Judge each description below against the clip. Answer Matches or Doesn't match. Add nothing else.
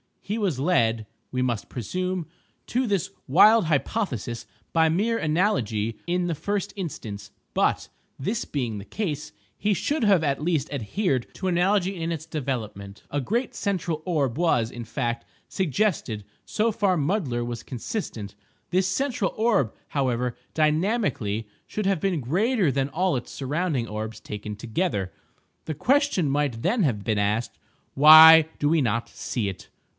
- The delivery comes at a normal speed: Matches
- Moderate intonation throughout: Doesn't match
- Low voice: Doesn't match